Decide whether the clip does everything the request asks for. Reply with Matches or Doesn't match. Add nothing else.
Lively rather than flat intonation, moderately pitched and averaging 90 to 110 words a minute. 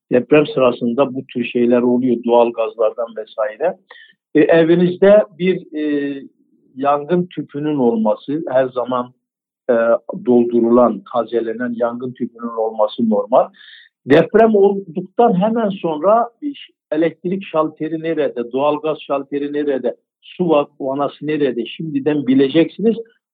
Matches